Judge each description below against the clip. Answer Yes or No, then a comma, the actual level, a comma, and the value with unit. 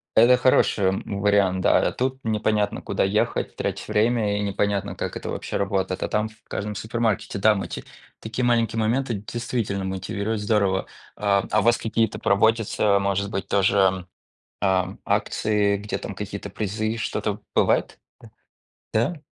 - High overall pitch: No, low, 105 Hz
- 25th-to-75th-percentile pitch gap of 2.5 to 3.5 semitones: No, narrow, 2.0 semitones